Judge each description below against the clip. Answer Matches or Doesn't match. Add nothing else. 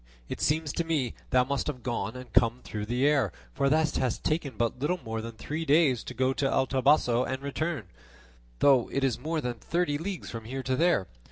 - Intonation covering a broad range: Doesn't match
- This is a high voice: Doesn't match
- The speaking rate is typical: Doesn't match